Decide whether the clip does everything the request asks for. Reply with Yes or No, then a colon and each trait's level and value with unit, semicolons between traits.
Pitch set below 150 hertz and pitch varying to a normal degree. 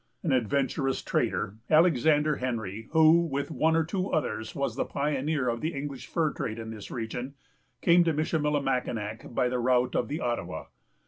Yes: medium, 140 Hz; average, 4.4 semitones